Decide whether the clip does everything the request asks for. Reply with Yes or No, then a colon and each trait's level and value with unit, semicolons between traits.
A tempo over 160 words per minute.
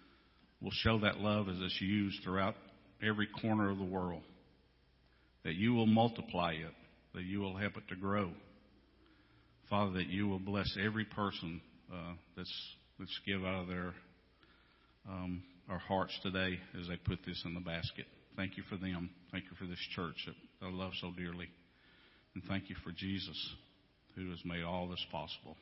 Yes: average, 175 wpm